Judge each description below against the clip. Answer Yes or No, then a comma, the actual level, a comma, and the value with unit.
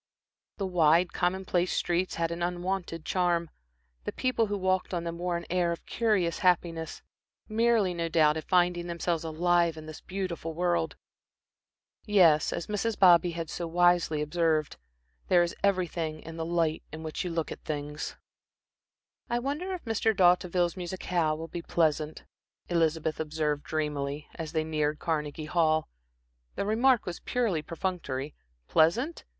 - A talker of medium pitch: Yes, medium, 170 Hz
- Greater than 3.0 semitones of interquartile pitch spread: No, narrow, 2.5 semitones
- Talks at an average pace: Yes, average, 150 wpm